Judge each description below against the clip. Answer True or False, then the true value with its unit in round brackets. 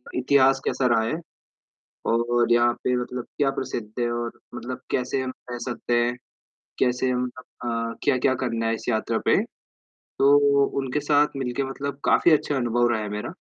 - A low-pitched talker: True (125 Hz)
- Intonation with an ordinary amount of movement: False (2.0 semitones)